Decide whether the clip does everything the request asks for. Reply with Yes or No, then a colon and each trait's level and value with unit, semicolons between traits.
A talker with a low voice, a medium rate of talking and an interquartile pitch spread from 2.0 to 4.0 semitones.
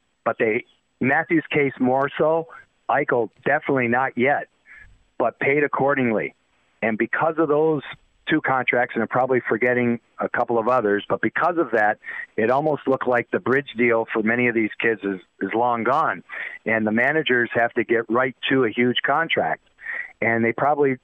Yes: low, 125 Hz; average, 175 wpm; average, 3.6 semitones